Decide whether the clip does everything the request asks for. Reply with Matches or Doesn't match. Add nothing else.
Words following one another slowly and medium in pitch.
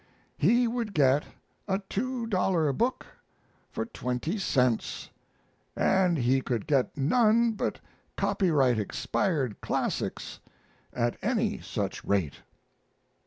Matches